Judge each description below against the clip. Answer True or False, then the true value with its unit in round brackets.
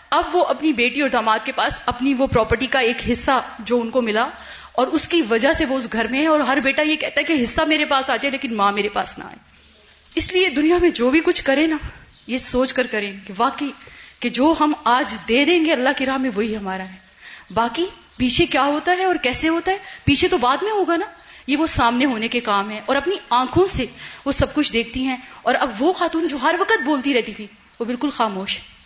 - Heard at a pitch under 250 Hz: False (270 Hz)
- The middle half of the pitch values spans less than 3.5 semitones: False (5.0 semitones)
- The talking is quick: True (250 wpm)